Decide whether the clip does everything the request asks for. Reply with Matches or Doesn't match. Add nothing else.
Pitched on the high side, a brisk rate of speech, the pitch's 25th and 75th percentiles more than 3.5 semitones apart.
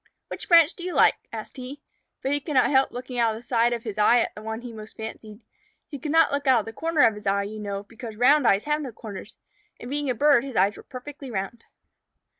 Matches